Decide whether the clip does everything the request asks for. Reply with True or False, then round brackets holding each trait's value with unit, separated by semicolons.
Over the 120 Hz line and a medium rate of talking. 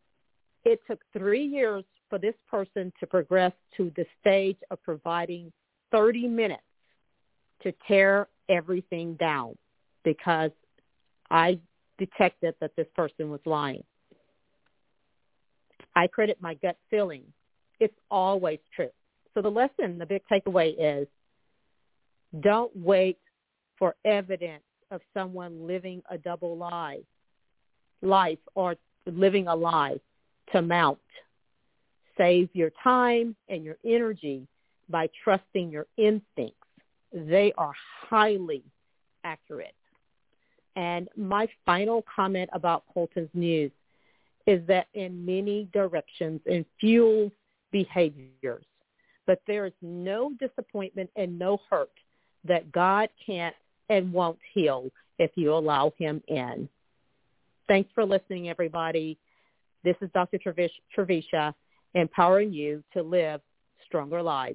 False (185 Hz; 115 wpm)